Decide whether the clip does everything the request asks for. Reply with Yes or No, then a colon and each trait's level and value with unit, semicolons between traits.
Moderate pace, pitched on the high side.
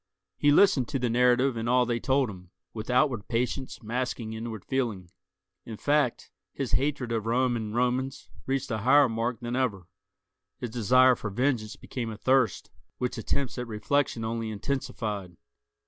No: average, 165 wpm; low, 120 Hz